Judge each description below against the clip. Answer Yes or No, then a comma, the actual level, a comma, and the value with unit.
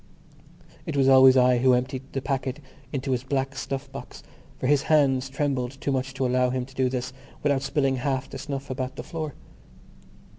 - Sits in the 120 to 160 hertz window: Yes, low, 135 Hz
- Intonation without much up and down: Yes, narrow, 1.2 semitones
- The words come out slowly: No, average, 190 wpm